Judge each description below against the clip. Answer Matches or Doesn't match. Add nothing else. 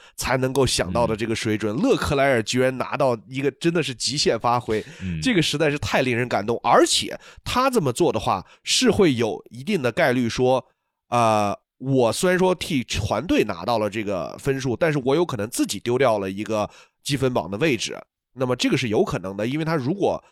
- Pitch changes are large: Doesn't match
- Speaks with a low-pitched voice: Matches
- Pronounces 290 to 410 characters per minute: Matches